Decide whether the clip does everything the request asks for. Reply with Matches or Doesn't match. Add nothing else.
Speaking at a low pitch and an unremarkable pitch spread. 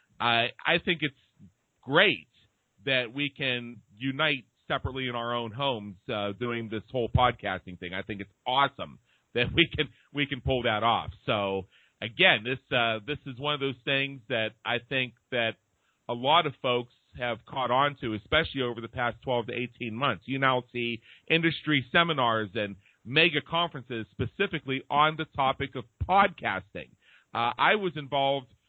Matches